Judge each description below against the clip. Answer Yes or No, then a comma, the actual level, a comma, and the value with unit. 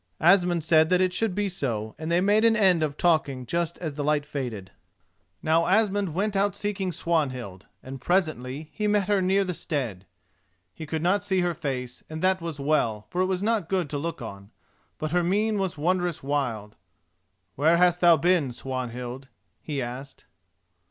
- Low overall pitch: No, medium, 165 Hz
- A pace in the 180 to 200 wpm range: Yes, average, 185 wpm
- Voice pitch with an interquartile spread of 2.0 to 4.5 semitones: No, wide, 5.4 semitones